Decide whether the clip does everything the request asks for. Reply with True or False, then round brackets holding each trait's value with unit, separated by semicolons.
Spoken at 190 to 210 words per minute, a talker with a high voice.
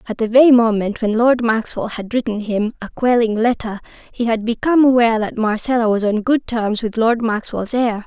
True (200 wpm; 230 Hz)